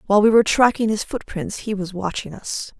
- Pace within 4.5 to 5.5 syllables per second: No, 5.8 syllables/s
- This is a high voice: Yes, high, 205 Hz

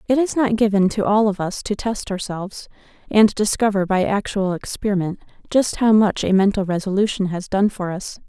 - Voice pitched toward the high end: Yes, high, 205 Hz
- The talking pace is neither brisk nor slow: Yes, average, 190 wpm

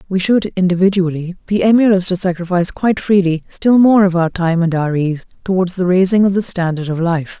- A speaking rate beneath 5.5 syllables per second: No, 5.7 syllables/s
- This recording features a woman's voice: Yes, female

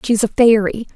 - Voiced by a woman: Yes, female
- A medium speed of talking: Yes, average, 190 wpm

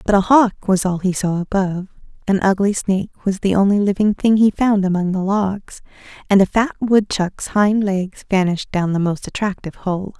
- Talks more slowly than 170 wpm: No, average, 195 wpm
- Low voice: No, high, 195 Hz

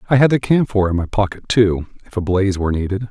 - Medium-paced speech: No, fast, 250 wpm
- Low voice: Yes, low, 100 Hz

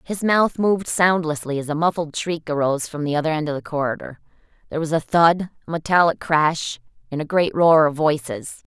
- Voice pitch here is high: No, medium, 160 Hz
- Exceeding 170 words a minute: Yes, average, 200 wpm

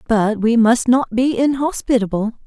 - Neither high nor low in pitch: No, high, 240 Hz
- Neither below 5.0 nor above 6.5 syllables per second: No, 4.4 syllables/s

